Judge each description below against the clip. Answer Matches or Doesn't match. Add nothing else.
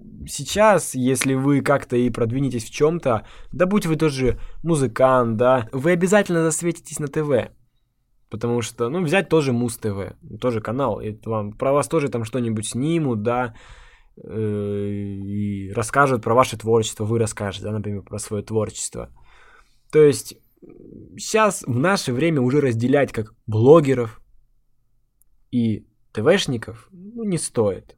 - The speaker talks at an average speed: Matches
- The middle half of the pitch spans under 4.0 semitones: Doesn't match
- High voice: Doesn't match